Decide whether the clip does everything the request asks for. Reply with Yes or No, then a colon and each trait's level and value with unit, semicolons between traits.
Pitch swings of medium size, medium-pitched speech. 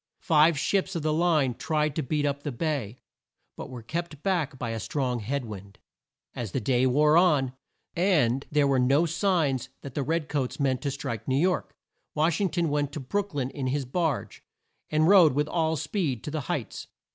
Yes: average, 3.8 semitones; medium, 145 Hz